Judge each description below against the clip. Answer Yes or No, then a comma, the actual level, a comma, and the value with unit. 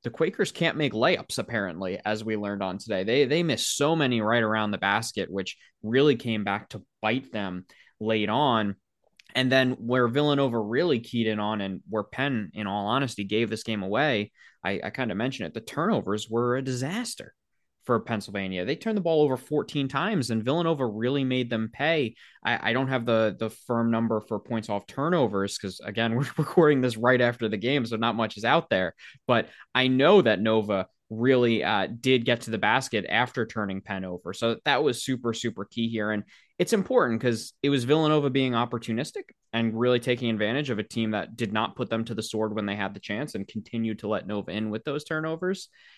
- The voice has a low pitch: Yes, low, 115 Hz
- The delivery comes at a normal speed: No, fast, 210 wpm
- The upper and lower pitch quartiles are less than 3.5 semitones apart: No, average, 3.8 semitones